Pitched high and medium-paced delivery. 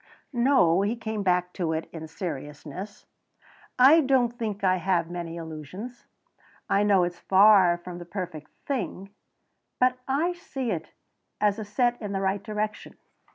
Yes: high, 195 Hz; average, 150 wpm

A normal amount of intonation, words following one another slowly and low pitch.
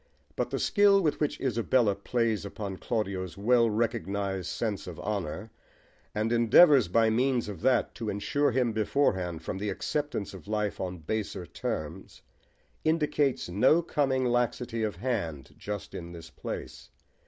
No: average, 4.6 semitones; average, 145 wpm; low, 110 Hz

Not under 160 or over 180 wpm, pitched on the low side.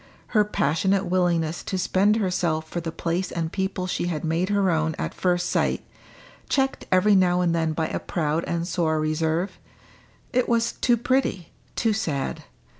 No: average, 170 wpm; medium, 175 Hz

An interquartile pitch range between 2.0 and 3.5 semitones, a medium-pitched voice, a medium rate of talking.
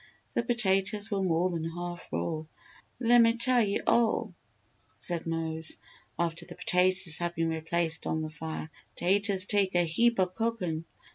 No: average, 4.0 semitones; medium, 180 Hz; average, 150 wpm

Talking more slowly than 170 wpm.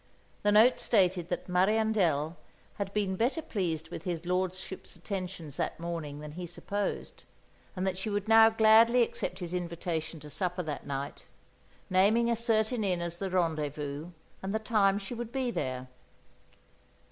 Yes: average, 160 wpm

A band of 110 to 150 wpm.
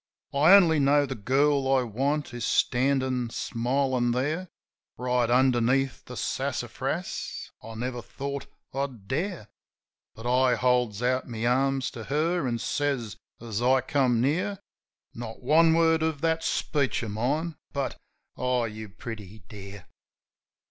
Yes: average, 140 wpm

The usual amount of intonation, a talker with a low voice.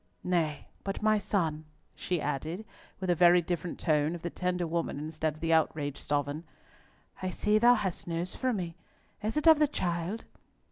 No: average, 3.8 semitones; medium, 175 Hz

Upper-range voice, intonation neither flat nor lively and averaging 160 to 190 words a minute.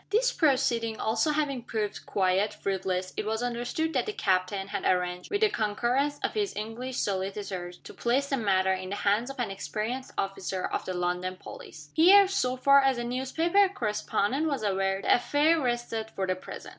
No: high, 225 Hz; wide, 6.1 semitones; average, 185 wpm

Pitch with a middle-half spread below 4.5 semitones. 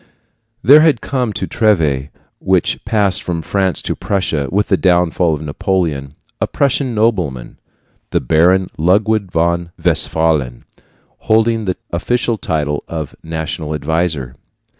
No: average, 5.2 semitones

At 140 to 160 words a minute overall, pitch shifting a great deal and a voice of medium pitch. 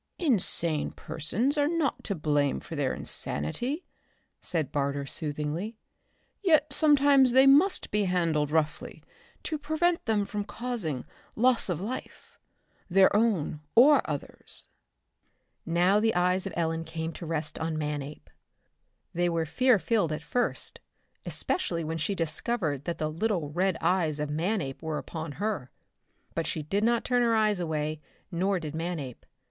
Yes: average, 145 wpm; wide, 6.8 semitones; medium, 175 Hz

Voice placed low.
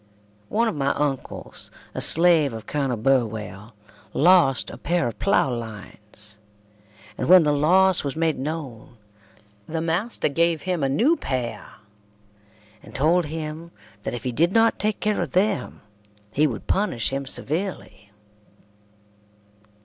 No: medium, 150 Hz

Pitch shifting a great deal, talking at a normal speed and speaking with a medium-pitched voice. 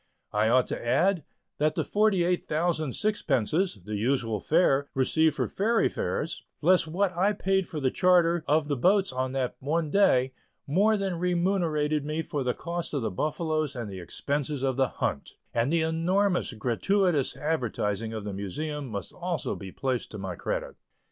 Yes: wide, 5.8 semitones; average, 175 wpm; medium, 155 Hz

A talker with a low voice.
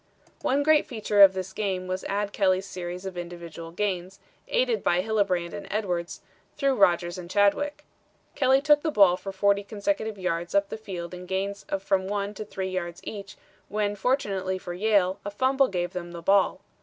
No: high, 195 Hz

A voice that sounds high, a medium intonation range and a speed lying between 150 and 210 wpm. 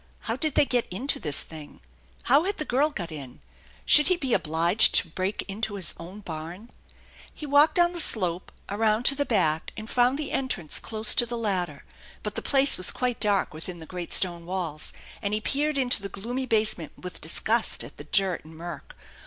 No: high, 210 Hz; wide, 6.7 semitones; average, 200 wpm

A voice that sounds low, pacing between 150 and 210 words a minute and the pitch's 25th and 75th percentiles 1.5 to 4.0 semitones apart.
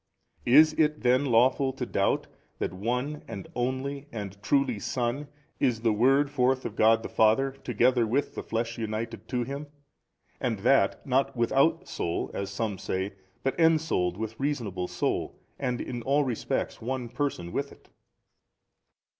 Yes: low, 125 Hz; average, 155 wpm; average, 3.5 semitones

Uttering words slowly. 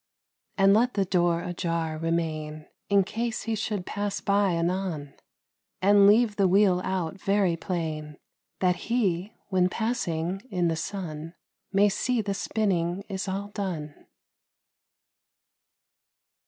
Yes: slow, 125 wpm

